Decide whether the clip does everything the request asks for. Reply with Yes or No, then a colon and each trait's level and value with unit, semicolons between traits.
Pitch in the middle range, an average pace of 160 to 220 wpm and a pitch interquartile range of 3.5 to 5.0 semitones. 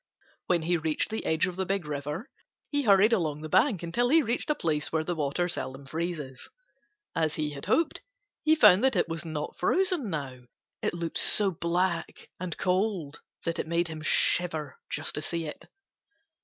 Yes: medium, 170 Hz; average, 185 wpm; average, 4.0 semitones